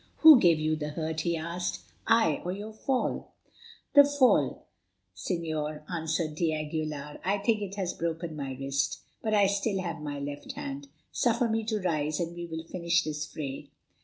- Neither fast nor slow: Yes, average, 175 wpm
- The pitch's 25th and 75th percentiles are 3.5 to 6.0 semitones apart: Yes, average, 4.5 semitones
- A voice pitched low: No, medium, 165 Hz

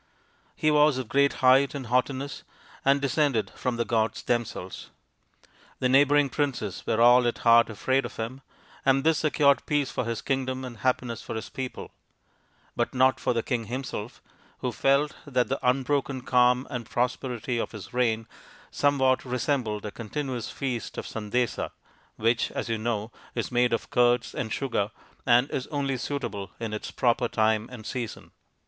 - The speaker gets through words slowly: No, average, 165 wpm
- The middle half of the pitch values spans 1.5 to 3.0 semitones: Yes, average, 2.7 semitones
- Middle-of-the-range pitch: No, low, 125 Hz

